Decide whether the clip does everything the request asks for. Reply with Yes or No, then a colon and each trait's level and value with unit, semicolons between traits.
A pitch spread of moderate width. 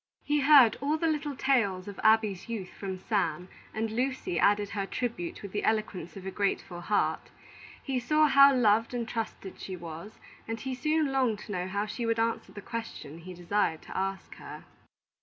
Yes: average, 5.0 semitones